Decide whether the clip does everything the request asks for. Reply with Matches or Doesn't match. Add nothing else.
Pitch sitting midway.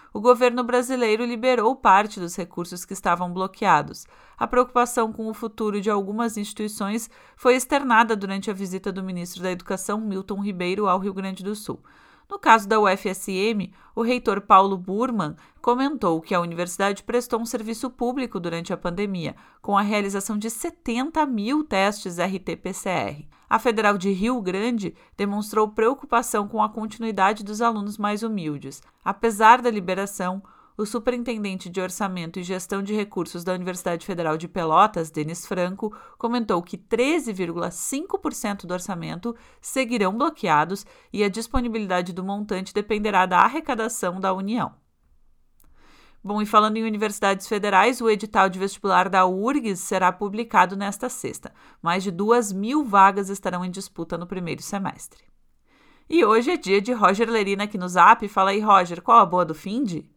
Doesn't match